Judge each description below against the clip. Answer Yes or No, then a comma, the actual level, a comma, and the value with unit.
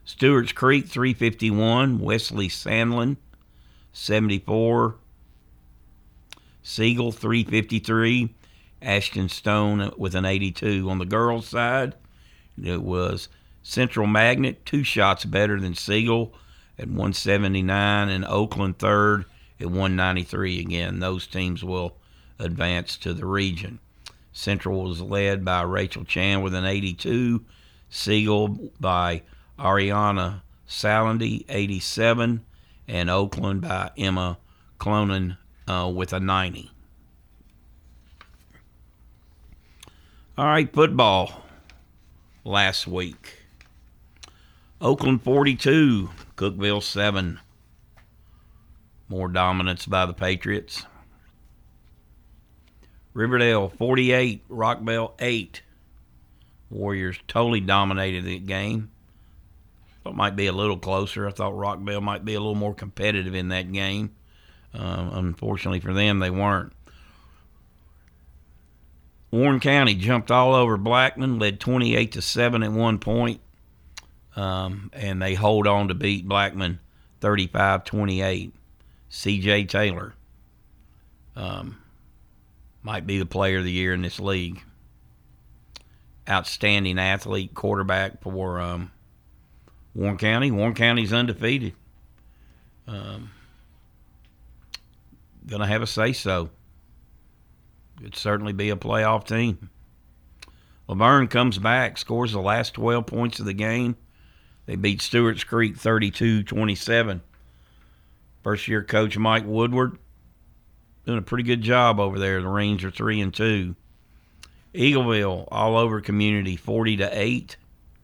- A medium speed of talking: No, slow, 110 wpm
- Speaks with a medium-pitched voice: No, very low, 95 Hz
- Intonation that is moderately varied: Yes, average, 4.0 semitones